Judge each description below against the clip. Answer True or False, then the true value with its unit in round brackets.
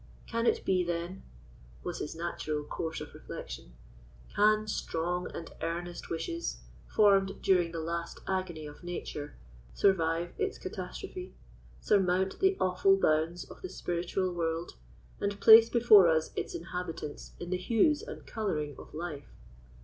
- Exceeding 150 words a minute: False (135 wpm)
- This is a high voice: False (175 Hz)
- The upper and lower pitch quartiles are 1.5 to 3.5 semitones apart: True (3.2 semitones)